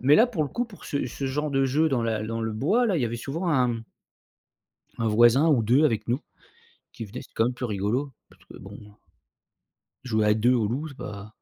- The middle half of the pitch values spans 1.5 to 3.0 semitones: No, average, 4.5 semitones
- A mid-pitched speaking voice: No, low, 125 Hz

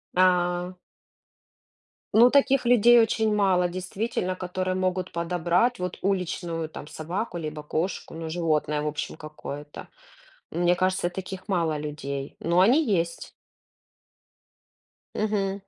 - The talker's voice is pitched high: No, medium, 180 Hz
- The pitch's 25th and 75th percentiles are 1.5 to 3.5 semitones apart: Yes, average, 2.9 semitones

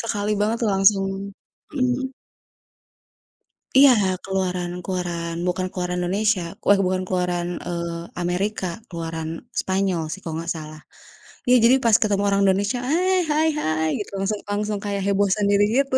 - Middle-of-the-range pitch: No, high, 195 Hz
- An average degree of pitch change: Yes, average, 3.1 semitones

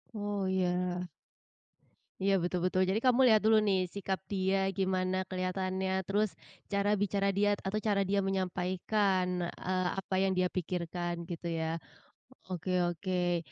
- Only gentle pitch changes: Yes, narrow, 1.6 semitones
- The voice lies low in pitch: No, high, 190 Hz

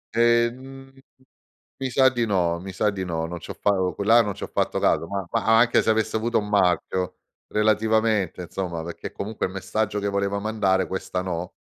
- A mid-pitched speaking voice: No, low, 100 Hz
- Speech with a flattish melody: No, average, 3.2 semitones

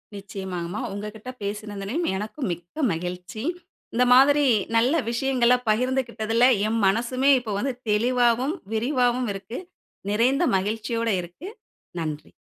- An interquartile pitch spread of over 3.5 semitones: Yes, average, 4.0 semitones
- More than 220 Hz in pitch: Yes, high, 230 Hz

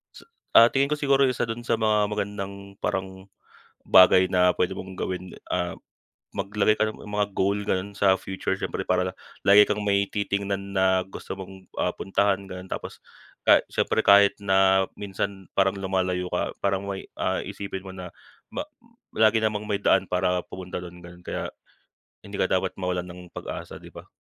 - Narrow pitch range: Yes, narrow, 1.6 semitones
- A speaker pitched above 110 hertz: No, very low, 95 Hz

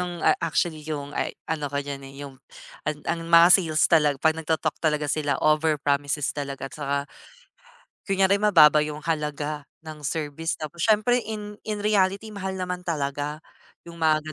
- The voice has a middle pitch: Yes, medium, 155 Hz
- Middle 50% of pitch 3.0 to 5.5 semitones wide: Yes, average, 3.4 semitones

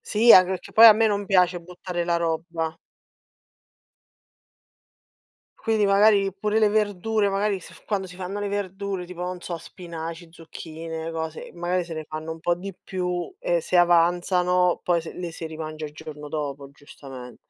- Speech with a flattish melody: No, average, 3.3 semitones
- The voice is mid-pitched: Yes, medium, 180 Hz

